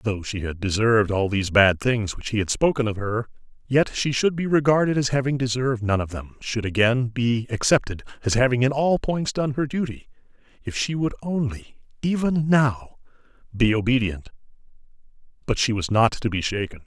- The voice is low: Yes, low, 120 Hz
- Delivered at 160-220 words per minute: Yes, average, 185 wpm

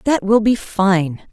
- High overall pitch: Yes, high, 205 Hz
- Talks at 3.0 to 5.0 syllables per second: Yes, 3.6 syllables/s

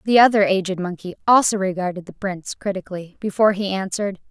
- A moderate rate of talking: Yes, average, 165 wpm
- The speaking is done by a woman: Yes, female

